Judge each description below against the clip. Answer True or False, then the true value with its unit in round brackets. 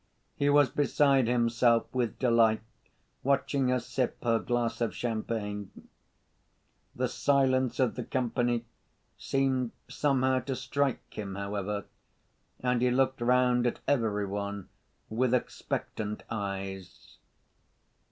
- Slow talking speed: True (115 wpm)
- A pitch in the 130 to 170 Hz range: False (120 Hz)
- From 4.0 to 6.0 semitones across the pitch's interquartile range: False (3.0 semitones)